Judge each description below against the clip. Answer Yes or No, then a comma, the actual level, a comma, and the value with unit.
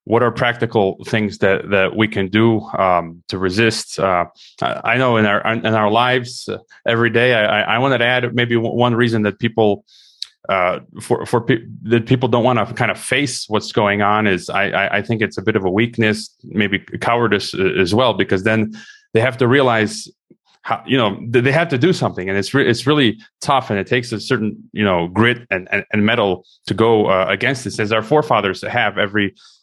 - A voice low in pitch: Yes, low, 110 Hz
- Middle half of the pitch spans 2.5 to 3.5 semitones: Yes, average, 2.9 semitones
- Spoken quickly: Yes, fast, 210 wpm